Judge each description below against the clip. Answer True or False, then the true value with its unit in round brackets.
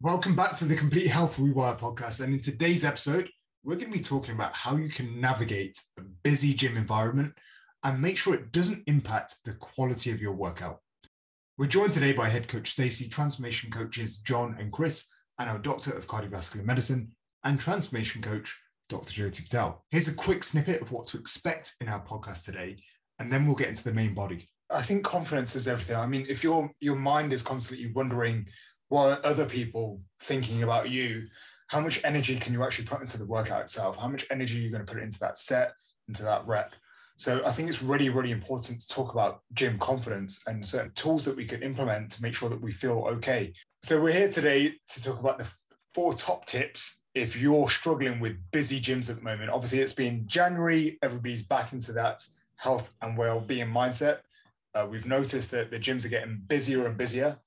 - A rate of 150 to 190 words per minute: False (205 wpm)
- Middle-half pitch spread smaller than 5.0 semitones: True (4.0 semitones)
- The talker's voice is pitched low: True (130 Hz)